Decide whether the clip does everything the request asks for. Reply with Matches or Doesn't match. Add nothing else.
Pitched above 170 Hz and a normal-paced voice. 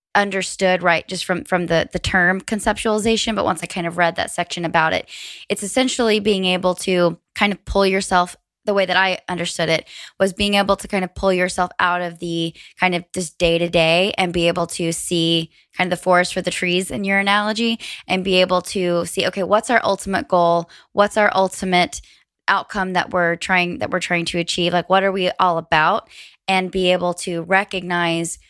Doesn't match